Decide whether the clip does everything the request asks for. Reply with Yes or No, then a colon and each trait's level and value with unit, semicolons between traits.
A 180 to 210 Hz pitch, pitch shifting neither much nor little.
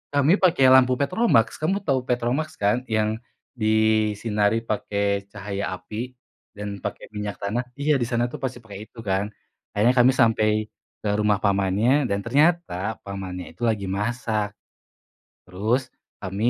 No: low, 110 Hz; average, 3.7 semitones